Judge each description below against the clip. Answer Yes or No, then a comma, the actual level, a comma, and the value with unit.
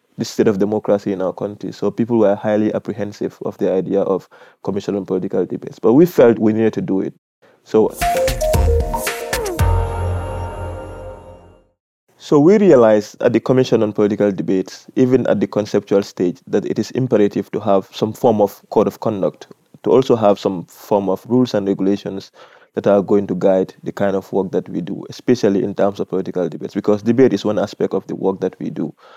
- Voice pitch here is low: Yes, low, 100 Hz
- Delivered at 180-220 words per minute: Yes, average, 190 wpm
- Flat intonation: Yes, narrow, 2.2 semitones